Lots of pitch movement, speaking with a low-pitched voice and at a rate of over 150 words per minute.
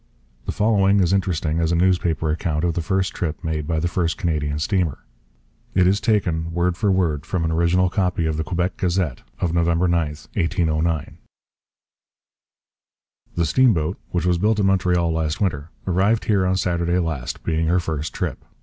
No: narrow, 2.5 semitones; very low, 85 Hz; average, 175 wpm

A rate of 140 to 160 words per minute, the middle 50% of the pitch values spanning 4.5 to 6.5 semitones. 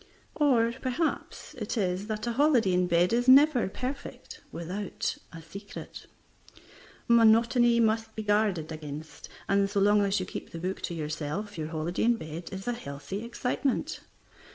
Yes: average, 155 wpm; average, 5.2 semitones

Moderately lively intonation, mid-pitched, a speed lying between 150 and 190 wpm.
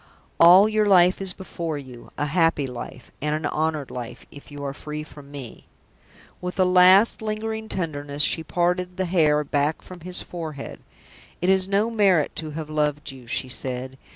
Yes: average, 4.2 semitones; medium, 160 Hz; average, 180 wpm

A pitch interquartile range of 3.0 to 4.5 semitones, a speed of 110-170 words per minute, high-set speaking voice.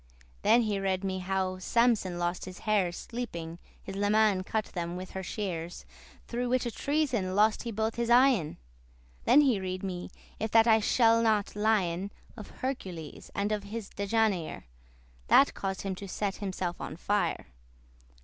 Yes: average, 3.4 semitones; average, 160 wpm; high, 200 Hz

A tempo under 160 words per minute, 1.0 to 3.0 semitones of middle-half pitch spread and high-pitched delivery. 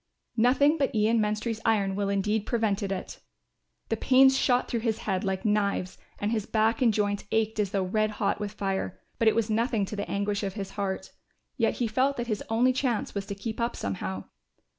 No: fast, 205 wpm; narrow, 2.4 semitones; high, 215 Hz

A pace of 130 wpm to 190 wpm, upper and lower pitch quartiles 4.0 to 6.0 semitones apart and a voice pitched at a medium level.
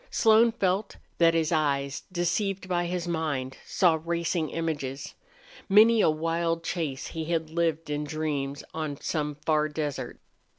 No: average, 140 wpm; narrow, 2.6 semitones; medium, 160 Hz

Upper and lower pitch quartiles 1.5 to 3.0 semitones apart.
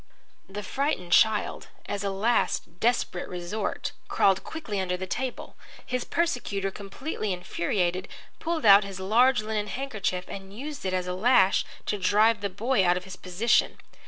No: average, 4.2 semitones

